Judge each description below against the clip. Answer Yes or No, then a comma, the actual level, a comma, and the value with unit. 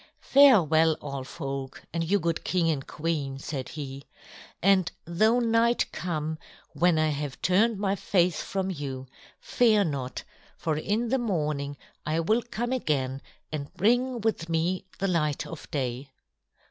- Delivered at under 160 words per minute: Yes, average, 145 wpm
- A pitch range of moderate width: No, wide, 5.9 semitones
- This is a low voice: No, medium, 165 Hz